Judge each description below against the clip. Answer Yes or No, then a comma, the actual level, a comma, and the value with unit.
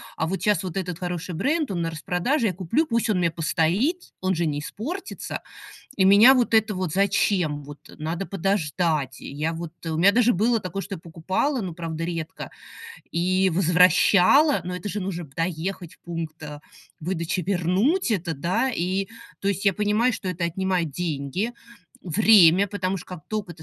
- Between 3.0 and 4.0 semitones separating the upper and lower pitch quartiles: Yes, average, 3.6 semitones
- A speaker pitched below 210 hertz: Yes, medium, 185 Hz